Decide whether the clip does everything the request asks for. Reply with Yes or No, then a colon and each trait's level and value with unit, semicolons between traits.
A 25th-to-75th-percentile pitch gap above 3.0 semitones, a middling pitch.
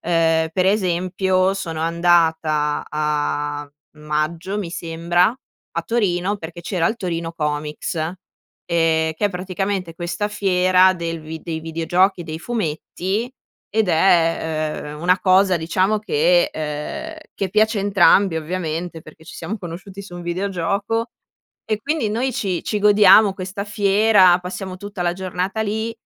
Yes: average, 3.5 semitones; medium, 180 Hz